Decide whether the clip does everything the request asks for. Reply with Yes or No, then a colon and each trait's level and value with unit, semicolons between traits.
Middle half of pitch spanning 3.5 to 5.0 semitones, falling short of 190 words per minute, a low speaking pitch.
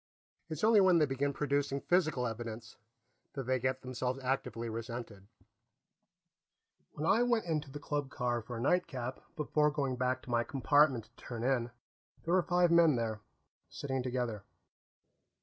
Yes: average, 3.9 semitones; average, 155 wpm; low, 130 Hz